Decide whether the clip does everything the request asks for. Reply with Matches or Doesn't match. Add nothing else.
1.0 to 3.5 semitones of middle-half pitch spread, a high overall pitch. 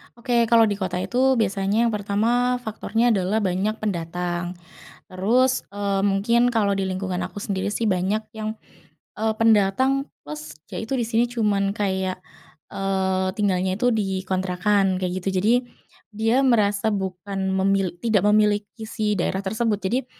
Matches